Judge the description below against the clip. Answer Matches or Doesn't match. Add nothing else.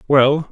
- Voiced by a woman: Doesn't match